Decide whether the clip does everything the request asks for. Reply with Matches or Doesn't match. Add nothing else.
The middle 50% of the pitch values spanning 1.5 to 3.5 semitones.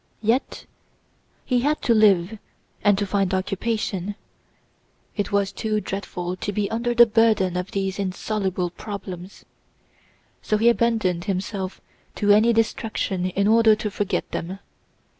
Matches